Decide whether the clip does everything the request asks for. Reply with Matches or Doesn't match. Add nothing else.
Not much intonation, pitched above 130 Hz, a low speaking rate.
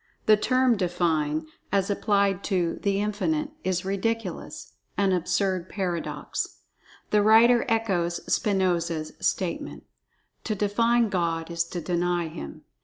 Doesn't match